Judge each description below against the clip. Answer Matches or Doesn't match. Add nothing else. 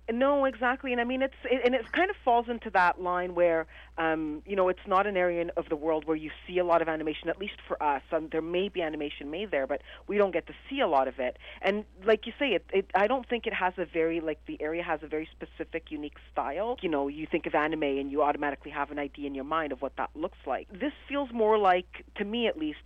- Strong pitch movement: Matches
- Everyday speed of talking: Doesn't match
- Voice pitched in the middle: Matches